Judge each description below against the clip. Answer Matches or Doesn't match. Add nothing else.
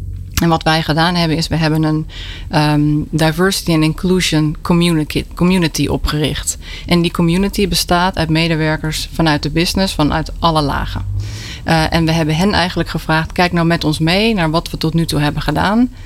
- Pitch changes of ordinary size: Doesn't match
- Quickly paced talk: Doesn't match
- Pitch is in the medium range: Matches